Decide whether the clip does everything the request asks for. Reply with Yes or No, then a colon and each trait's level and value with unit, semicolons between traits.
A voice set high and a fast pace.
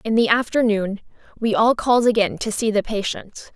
No: high, 220 Hz; average, 185 wpm